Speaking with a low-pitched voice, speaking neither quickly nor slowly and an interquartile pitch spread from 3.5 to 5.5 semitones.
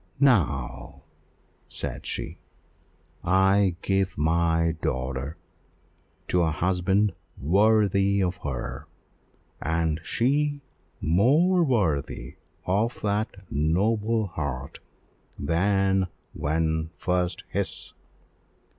No: very low, 90 Hz; slow, 80 wpm; average, 4.4 semitones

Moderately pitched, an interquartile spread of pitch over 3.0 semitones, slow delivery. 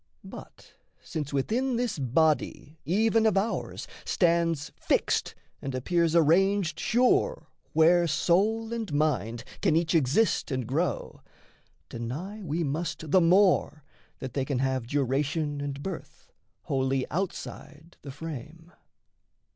Yes: medium, 160 Hz; average, 5.0 semitones; slow, 120 wpm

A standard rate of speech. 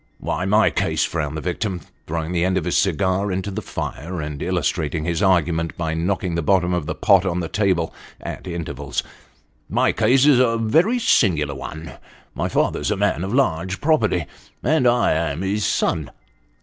Yes: average, 190 wpm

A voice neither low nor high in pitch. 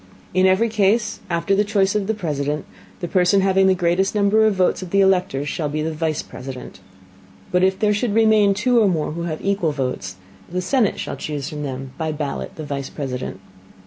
Yes: medium, 180 Hz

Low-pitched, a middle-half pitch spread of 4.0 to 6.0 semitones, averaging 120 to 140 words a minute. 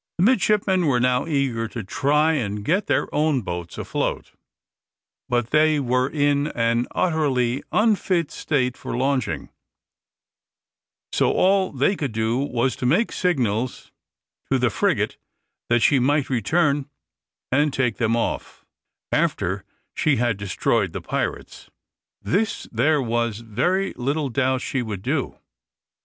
Yes: low, 130 Hz; average, 4.6 semitones; slow, 135 wpm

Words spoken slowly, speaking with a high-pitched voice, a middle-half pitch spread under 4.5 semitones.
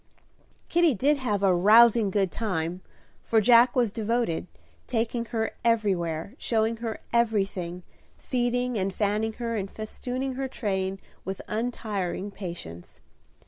Yes: slow, 125 wpm; high, 220 Hz; average, 3.7 semitones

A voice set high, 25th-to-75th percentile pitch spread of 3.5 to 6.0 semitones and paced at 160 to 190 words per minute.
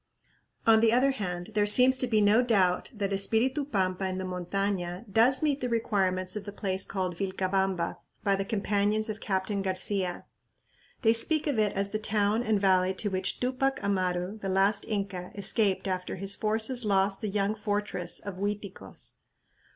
No: high, 200 Hz; average, 2.7 semitones; average, 175 wpm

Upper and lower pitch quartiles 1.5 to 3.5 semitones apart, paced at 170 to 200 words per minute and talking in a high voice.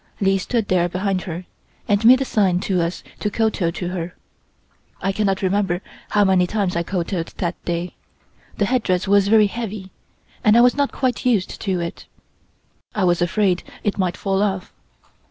Yes: average, 2.8 semitones; average, 175 wpm; high, 195 Hz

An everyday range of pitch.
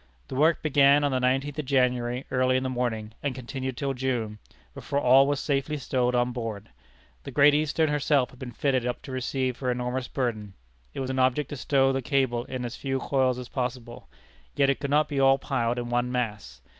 No: narrow, 2.0 semitones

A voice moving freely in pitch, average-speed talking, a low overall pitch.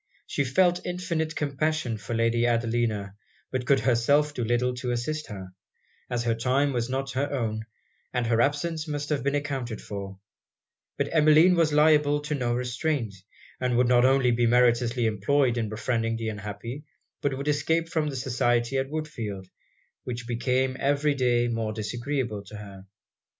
No: average, 3.8 semitones; average, 165 wpm; low, 125 Hz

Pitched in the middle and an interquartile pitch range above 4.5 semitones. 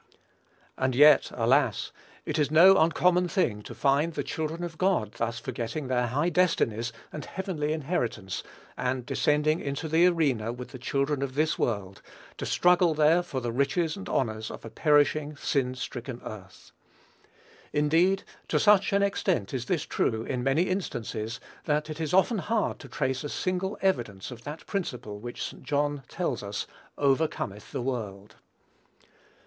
Yes: medium, 145 Hz; wide, 5.5 semitones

